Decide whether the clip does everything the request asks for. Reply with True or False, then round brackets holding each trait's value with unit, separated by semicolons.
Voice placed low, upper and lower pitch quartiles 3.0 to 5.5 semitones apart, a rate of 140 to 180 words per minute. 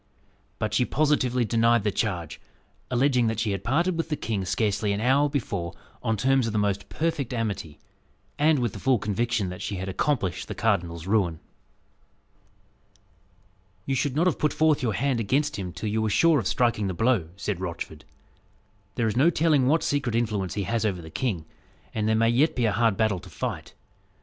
False (115 Hz; 5.0 semitones; 195 wpm)